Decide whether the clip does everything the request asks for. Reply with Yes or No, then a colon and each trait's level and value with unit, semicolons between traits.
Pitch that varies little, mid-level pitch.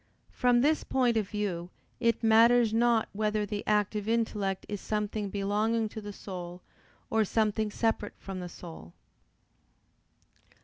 No: narrow, 2.0 semitones; high, 210 Hz